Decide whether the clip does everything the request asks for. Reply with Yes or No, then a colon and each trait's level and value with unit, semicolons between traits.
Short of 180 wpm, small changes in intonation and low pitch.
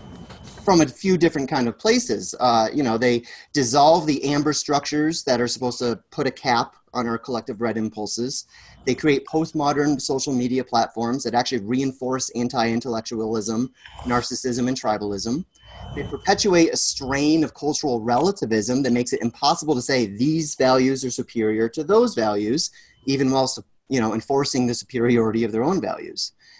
No: average, 160 wpm; average, 3.9 semitones; low, 130 Hz